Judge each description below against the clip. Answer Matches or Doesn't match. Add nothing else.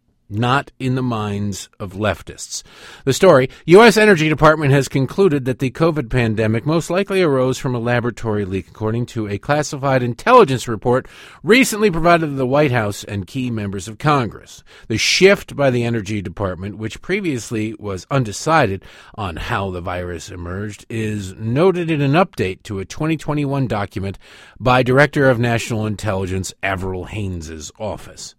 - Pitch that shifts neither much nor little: Doesn't match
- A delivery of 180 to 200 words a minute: Doesn't match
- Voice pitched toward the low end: Matches